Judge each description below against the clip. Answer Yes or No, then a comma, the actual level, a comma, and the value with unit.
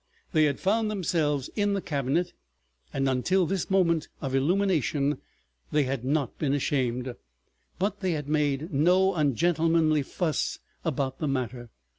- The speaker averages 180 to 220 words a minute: No, average, 140 wpm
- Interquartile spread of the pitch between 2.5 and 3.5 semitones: No, average, 4.6 semitones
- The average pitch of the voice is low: No, medium, 150 Hz